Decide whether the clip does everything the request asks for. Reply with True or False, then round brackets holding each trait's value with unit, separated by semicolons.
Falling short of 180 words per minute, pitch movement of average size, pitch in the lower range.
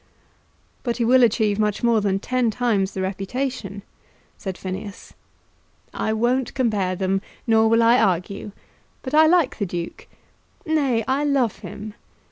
False (145 wpm; 4.2 semitones; 220 Hz)